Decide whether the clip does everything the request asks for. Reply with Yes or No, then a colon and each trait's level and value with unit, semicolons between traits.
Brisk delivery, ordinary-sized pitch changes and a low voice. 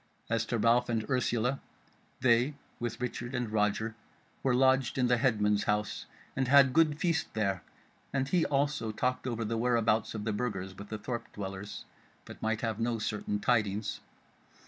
No: average, 170 wpm; average, 3.1 semitones; low, 115 Hz